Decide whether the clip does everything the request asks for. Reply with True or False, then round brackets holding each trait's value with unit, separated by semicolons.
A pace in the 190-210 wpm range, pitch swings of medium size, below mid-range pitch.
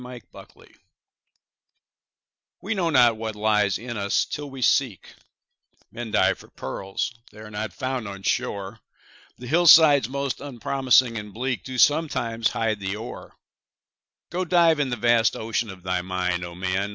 False (150 wpm; 4.6 semitones; 115 Hz)